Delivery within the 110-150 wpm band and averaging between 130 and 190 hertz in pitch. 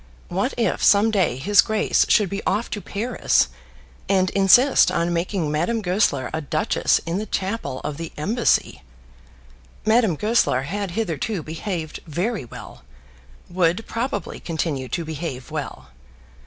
Yes: average, 140 wpm; medium, 185 Hz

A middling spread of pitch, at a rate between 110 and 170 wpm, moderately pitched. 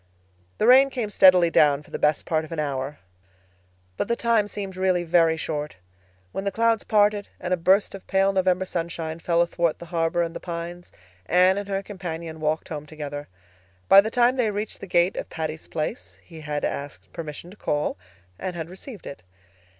No: average, 3.8 semitones; average, 195 wpm; medium, 175 Hz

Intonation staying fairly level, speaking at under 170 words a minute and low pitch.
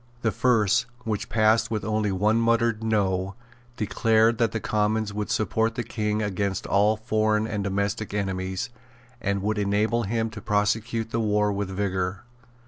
Yes: narrow, 1.8 semitones; average, 155 wpm; low, 105 Hz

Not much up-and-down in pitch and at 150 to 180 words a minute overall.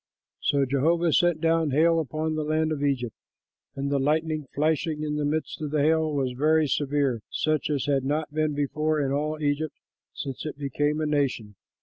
No: narrow, 1.8 semitones; average, 195 wpm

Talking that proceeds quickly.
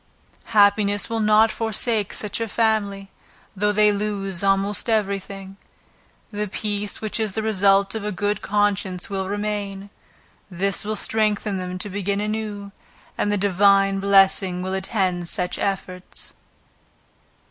No: slow, 135 wpm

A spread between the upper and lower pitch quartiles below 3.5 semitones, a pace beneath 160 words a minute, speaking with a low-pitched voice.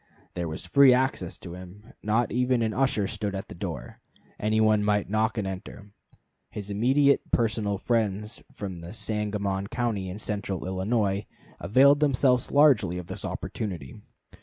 No: average, 3.8 semitones; average, 150 wpm; low, 105 Hz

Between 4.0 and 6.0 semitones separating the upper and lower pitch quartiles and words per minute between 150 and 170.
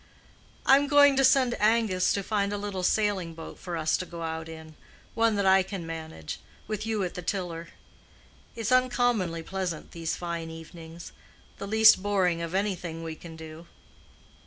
Yes: average, 4.3 semitones; average, 165 wpm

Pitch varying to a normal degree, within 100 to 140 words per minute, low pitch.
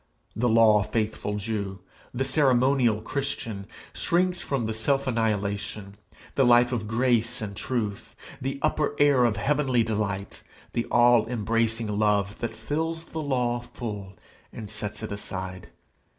Yes: average, 3.5 semitones; slow, 135 wpm; low, 115 Hz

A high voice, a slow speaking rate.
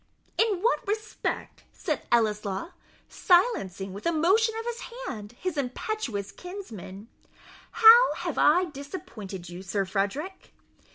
Yes: very high, 295 Hz; slow, 120 wpm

